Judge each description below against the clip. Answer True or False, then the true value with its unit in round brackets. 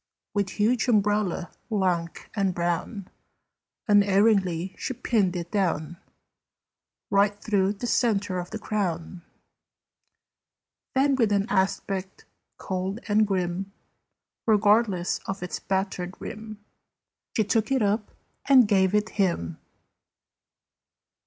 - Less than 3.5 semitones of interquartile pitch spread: True (2.5 semitones)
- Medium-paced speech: False (105 wpm)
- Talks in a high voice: True (200 Hz)